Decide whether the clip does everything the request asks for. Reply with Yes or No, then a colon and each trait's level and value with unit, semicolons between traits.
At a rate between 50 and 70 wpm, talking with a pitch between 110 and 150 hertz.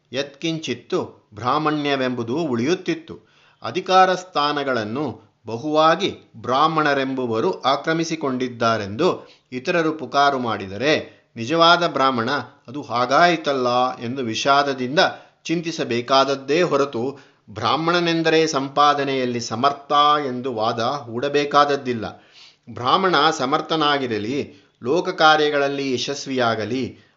Yes: slow, 65 wpm; medium, 140 Hz